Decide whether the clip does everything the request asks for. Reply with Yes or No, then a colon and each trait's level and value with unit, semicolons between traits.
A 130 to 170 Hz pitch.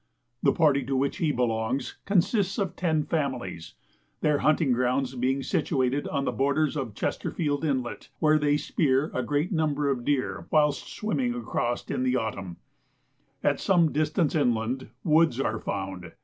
Yes: medium, 140 Hz